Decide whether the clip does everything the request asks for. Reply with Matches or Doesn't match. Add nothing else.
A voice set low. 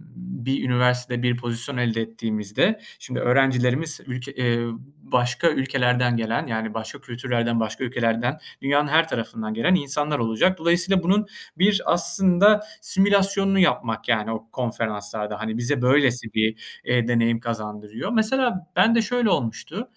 Matches